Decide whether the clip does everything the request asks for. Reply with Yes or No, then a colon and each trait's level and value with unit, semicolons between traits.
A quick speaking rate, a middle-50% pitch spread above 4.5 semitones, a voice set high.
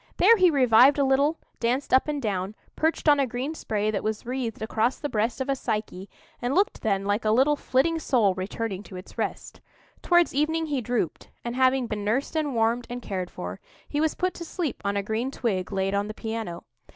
Yes: fast, 215 wpm; average, 5.1 semitones; high, 240 Hz